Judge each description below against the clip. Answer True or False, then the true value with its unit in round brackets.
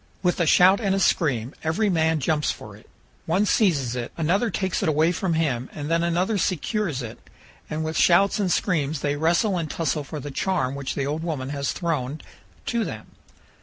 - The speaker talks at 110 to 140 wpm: False (200 wpm)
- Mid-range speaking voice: True (160 Hz)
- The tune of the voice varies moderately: True (4.1 semitones)